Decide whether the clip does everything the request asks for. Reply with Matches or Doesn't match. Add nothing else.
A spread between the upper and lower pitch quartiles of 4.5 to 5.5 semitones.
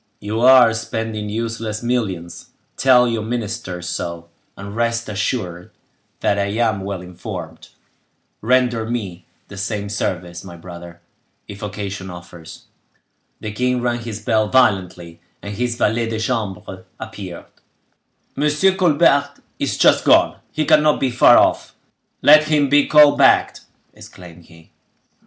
Matches